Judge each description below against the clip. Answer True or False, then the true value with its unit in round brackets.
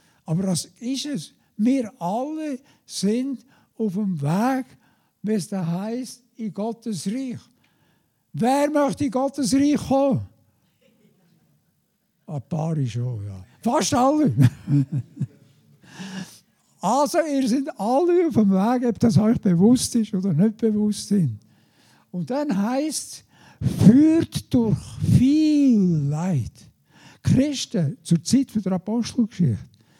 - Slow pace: True (115 wpm)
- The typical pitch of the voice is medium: False (215 Hz)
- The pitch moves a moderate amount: False (7.5 semitones)